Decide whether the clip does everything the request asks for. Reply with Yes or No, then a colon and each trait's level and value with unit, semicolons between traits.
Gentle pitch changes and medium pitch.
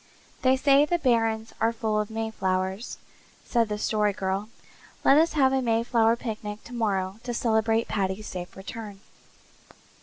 No: narrow, 2.3 semitones; high, 225 Hz